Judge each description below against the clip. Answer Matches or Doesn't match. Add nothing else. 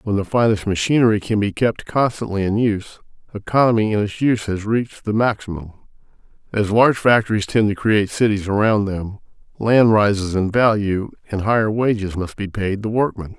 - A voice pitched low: Matches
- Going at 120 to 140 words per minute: Doesn't match